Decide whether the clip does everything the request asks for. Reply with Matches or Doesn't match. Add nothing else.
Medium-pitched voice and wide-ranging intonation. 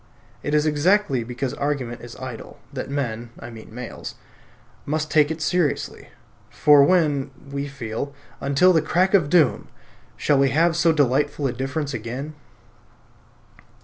Doesn't match